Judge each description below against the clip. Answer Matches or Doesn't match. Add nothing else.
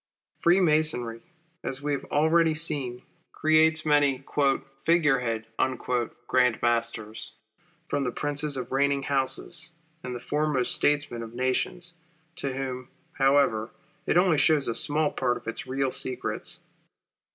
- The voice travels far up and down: Doesn't match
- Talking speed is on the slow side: Matches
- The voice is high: Doesn't match